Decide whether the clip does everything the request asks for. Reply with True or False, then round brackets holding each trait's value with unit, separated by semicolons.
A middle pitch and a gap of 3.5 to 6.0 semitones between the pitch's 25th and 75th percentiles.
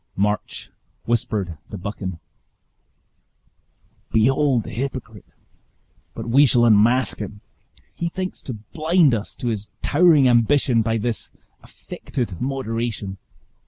False (115 Hz; 4.2 semitones)